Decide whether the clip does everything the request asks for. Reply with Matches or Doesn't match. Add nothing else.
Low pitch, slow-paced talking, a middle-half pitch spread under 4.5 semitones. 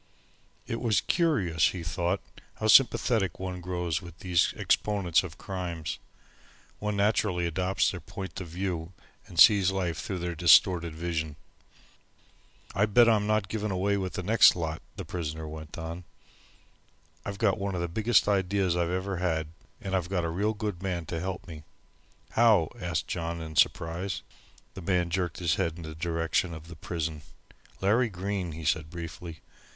Doesn't match